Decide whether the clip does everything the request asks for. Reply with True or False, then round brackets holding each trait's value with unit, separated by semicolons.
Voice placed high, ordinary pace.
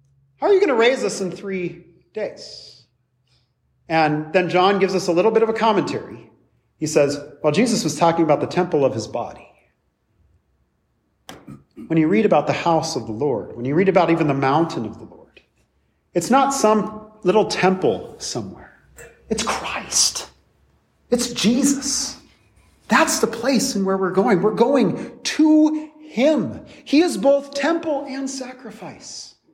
True (195 Hz; 165 wpm)